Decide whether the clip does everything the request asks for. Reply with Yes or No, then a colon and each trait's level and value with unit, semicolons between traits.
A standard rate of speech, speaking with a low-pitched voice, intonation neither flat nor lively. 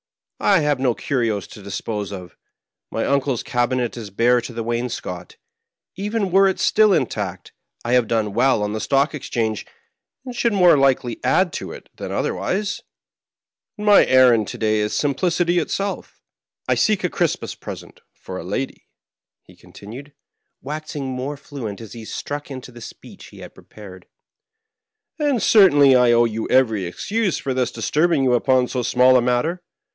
No: average, 170 wpm; low, 130 Hz; wide, 6.5 semitones